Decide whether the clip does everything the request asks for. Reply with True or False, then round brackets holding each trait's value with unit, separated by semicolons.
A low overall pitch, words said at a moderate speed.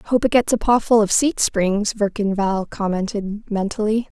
False (210 Hz; 185 wpm)